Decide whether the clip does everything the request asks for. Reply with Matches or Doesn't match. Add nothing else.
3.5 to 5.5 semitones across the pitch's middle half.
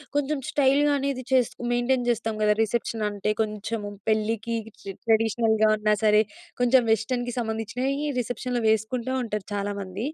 Doesn't match